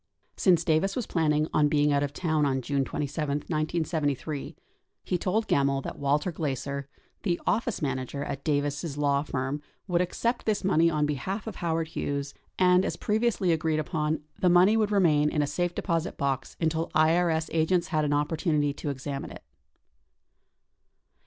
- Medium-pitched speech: Yes, medium, 155 Hz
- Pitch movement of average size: Yes, average, 3.5 semitones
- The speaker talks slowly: No, average, 165 wpm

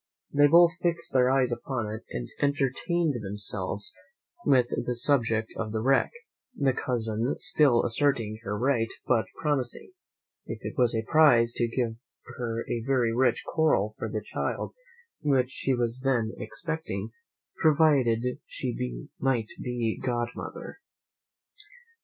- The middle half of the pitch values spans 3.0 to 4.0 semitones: Yes, average, 3.6 semitones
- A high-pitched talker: No, low, 125 Hz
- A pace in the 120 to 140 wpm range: Yes, slow, 135 wpm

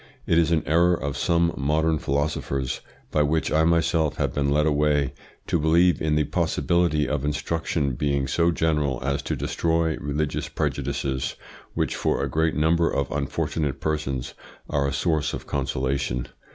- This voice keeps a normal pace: Yes, average, 160 wpm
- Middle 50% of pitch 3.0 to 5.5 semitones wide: No, narrow, 2.5 semitones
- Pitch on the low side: Yes, very low, 75 Hz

